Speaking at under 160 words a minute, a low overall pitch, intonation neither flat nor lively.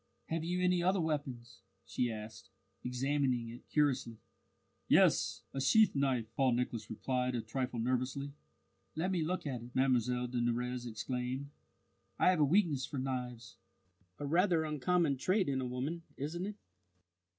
Yes: average, 150 wpm; low, 130 Hz; average, 4.2 semitones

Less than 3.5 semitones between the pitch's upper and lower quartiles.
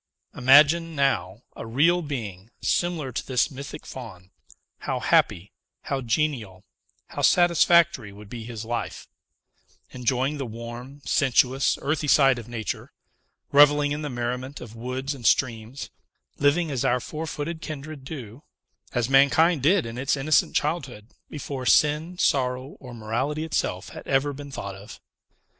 No: average, 3.9 semitones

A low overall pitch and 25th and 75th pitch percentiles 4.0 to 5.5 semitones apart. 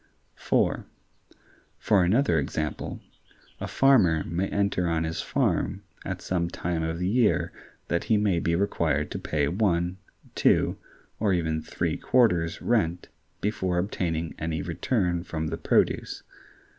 No: very low, 85 Hz; average, 3.5 semitones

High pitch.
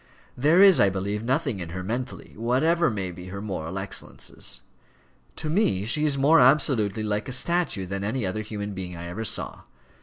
No: low, 110 Hz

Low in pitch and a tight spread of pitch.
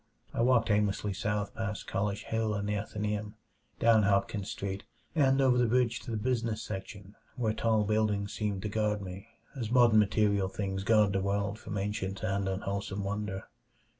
Yes: low, 105 Hz; narrow, 1.9 semitones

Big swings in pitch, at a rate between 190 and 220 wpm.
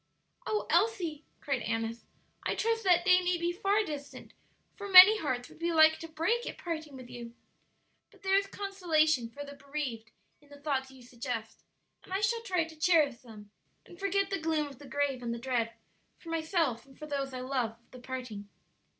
Yes: wide, 6.0 semitones; average, 200 wpm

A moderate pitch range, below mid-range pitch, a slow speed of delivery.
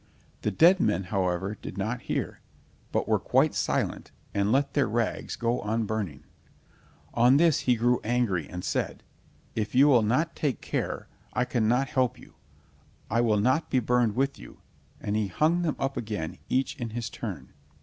No: average, 3.7 semitones; low, 120 Hz; average, 175 wpm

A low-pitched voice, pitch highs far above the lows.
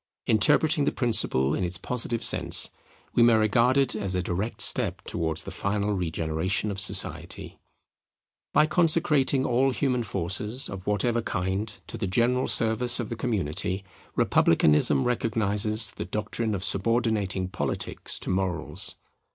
No: low, 110 Hz; average, 4.2 semitones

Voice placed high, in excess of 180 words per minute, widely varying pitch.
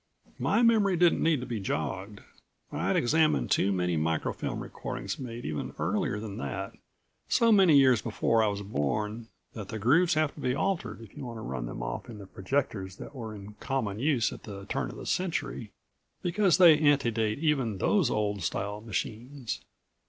No: low, 115 Hz; average, 190 wpm; wide, 6.5 semitones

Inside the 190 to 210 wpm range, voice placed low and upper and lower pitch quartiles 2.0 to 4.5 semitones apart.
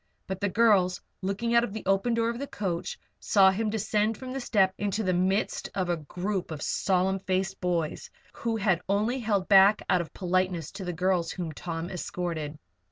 No: average, 195 wpm; high, 190 Hz; average, 2.9 semitones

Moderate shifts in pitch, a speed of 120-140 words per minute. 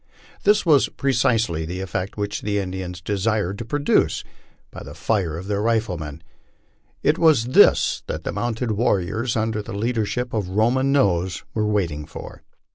No: average, 4.2 semitones; average, 165 wpm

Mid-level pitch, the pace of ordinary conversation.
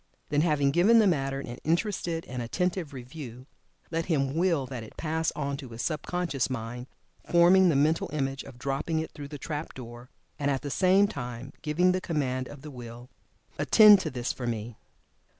Yes: medium, 145 Hz; average, 190 wpm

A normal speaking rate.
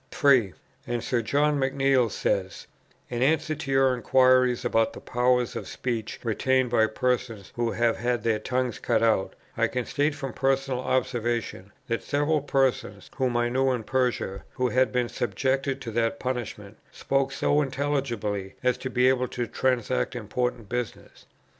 Yes: average, 160 wpm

